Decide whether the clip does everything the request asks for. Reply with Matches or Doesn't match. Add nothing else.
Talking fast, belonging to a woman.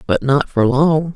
Matches